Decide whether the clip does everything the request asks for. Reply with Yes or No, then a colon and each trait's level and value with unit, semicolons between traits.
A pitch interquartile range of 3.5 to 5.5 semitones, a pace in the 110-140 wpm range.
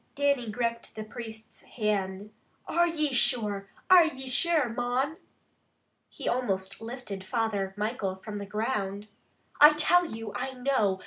Yes: average, 4.5 semitones; slow, 135 wpm